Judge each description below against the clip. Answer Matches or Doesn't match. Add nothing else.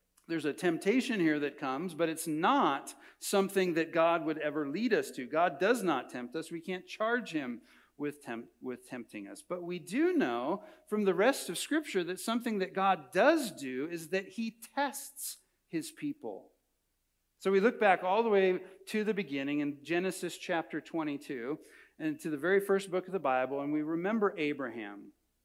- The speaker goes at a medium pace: Matches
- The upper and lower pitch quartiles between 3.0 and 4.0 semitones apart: Doesn't match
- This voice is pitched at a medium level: Matches